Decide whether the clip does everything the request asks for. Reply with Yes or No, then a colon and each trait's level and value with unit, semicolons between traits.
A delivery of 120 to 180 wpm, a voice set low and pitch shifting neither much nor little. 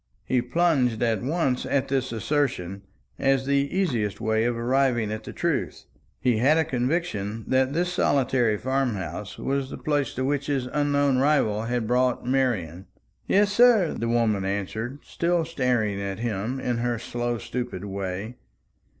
Yes: average, 160 wpm; low, 125 Hz; average, 4.1 semitones